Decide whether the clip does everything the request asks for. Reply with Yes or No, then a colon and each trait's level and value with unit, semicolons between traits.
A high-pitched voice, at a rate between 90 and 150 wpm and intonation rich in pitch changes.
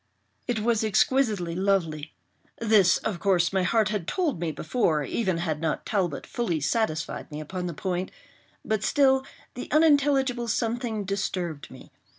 Yes: high, 195 Hz; average, 140 wpm; wide, 5.8 semitones